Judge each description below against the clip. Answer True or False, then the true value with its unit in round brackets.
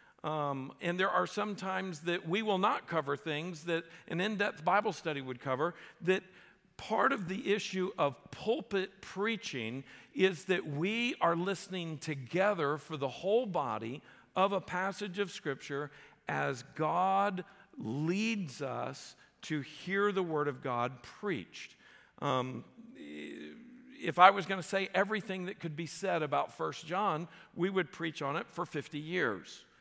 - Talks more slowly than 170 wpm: True (155 wpm)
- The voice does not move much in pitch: False (4.7 semitones)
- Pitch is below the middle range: False (180 Hz)